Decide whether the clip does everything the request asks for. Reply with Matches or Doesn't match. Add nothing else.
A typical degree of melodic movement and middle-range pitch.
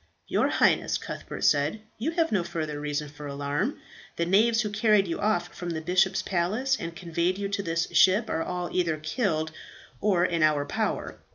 Matches